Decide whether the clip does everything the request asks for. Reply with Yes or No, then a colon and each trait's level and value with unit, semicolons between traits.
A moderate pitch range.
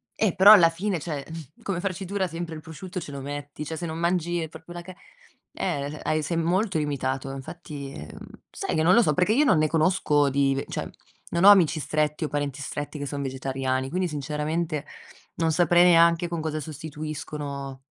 Yes: average, 3.2 semitones